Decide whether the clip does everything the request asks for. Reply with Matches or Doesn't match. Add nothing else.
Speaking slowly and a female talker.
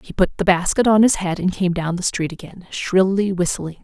Doesn't match